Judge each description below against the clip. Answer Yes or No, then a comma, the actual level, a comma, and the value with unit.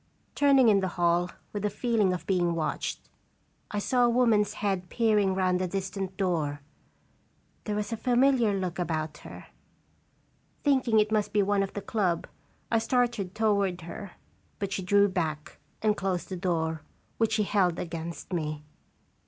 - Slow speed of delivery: No, average, 160 wpm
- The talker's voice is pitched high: Yes, high, 195 Hz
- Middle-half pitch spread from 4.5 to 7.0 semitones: No, average, 3.4 semitones